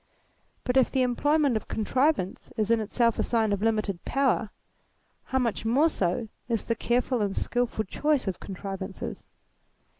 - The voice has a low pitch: No, high, 230 Hz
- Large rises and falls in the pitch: No, average, 3.8 semitones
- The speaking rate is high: No, average, 155 wpm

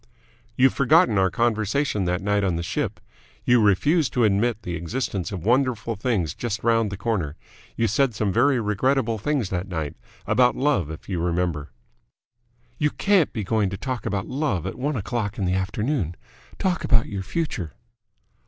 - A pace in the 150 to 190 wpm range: Yes, average, 170 wpm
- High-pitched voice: No, low, 110 Hz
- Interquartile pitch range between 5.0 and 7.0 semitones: Yes, average, 5.3 semitones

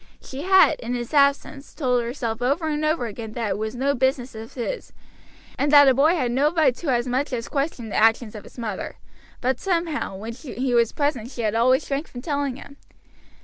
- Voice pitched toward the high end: Yes, very high, 260 Hz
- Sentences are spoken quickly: Yes, fast, 215 wpm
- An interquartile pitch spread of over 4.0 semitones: No, average, 3.5 semitones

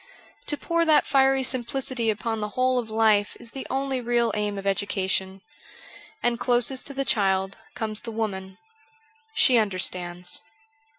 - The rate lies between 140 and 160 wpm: Yes, average, 155 wpm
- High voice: Yes, high, 230 Hz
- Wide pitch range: No, average, 4.7 semitones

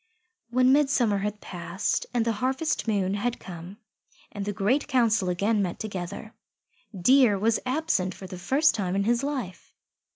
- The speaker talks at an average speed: Yes, average, 160 wpm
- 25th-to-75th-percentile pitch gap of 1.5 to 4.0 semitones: No, average, 4.8 semitones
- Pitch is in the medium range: No, high, 210 Hz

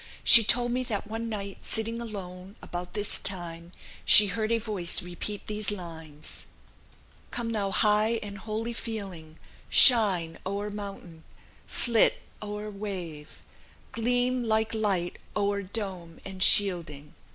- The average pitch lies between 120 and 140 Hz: No, high, 205 Hz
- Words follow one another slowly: Yes, slow, 130 wpm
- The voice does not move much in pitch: No, average, 3.6 semitones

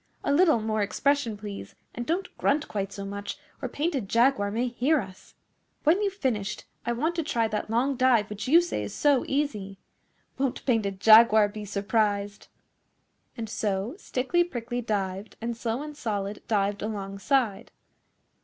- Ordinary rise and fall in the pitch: Yes, average, 5.0 semitones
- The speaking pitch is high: Yes, high, 225 Hz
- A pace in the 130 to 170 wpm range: Yes, average, 160 wpm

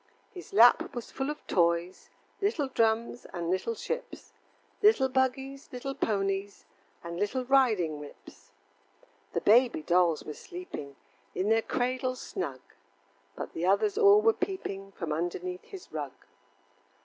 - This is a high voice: Yes, high, 230 Hz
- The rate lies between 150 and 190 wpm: No, slow, 135 wpm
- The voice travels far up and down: Yes, wide, 7.1 semitones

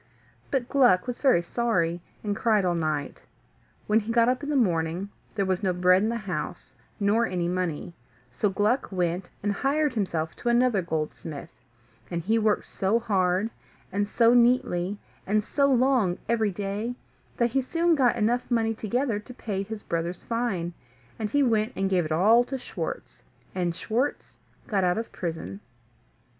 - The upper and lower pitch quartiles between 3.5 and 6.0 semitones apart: Yes, average, 4.9 semitones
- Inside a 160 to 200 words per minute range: Yes, average, 170 wpm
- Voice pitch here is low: No, high, 210 Hz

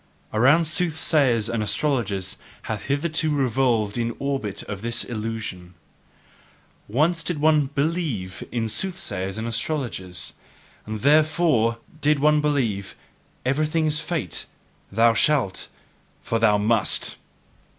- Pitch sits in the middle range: No, low, 125 Hz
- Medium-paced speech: No, slow, 110 wpm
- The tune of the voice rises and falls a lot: Yes, wide, 6.0 semitones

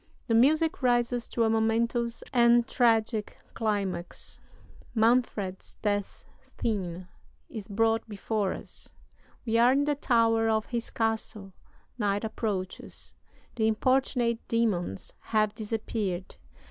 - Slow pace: Yes, slow, 110 wpm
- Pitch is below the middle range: No, high, 225 Hz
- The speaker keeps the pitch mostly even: Yes, narrow, 2.3 semitones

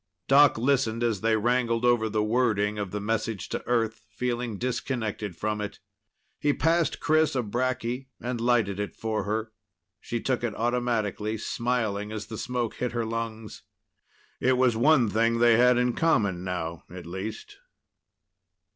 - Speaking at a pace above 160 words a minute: No, average, 155 wpm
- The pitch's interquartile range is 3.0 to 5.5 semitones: No, narrow, 2.6 semitones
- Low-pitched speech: Yes, low, 115 Hz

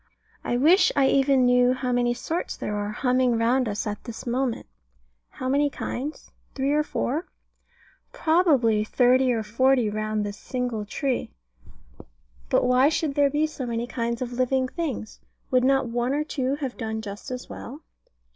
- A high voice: Yes, very high, 255 Hz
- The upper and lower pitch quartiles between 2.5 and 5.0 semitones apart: Yes, average, 2.8 semitones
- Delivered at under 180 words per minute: Yes, average, 170 wpm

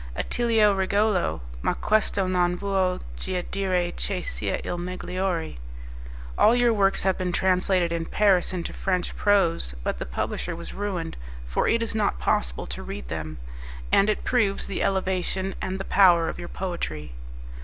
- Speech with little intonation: Yes, narrow, 2.3 semitones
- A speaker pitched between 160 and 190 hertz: Yes, medium, 185 Hz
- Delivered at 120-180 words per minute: Yes, average, 160 wpm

